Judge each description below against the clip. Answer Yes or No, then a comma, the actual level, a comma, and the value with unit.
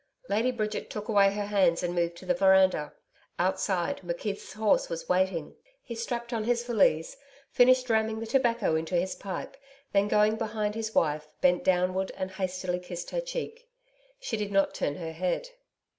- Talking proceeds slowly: No, average, 175 wpm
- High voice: Yes, high, 200 Hz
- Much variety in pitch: No, average, 3.9 semitones